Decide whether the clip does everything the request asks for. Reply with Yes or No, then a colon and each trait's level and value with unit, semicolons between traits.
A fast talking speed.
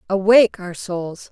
No: slow, 135 wpm